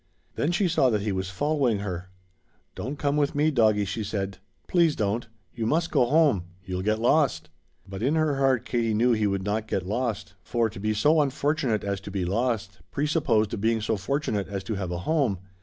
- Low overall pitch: Yes, low, 110 Hz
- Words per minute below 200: No, fast, 205 wpm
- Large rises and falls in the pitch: Yes, wide, 6.0 semitones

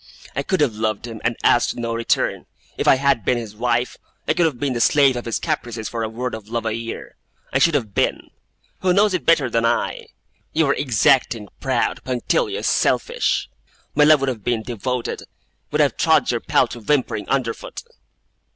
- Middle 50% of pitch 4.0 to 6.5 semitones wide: No, average, 3.5 semitones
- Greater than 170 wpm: Yes, average, 195 wpm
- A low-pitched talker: Yes, low, 120 Hz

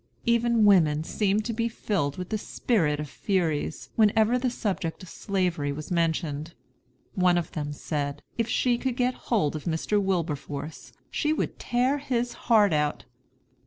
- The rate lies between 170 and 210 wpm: No, average, 160 wpm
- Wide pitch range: Yes, wide, 7.0 semitones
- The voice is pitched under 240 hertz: Yes, high, 190 Hz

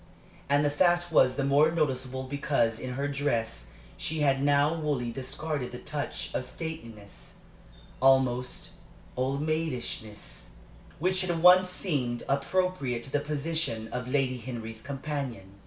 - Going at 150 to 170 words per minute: No, slow, 135 wpm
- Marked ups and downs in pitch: No, average, 3.6 semitones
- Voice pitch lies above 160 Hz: No, medium, 140 Hz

